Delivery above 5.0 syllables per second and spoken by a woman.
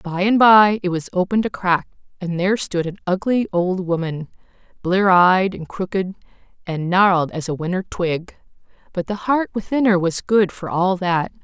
No: 4.8 syllables/s; female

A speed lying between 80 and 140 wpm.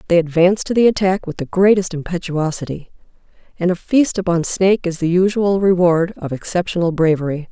No: average, 170 wpm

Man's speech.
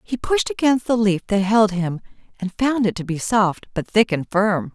No: female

